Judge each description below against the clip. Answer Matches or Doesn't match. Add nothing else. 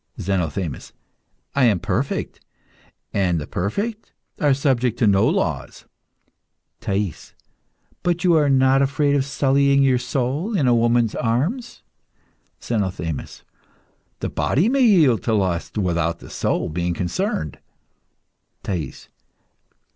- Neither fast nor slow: Doesn't match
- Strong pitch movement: Matches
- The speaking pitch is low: Matches